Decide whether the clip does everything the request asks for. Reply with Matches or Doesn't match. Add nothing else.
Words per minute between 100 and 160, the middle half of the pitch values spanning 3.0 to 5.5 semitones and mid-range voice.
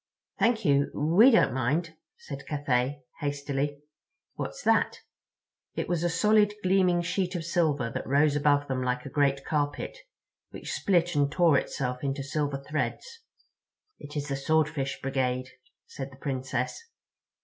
Matches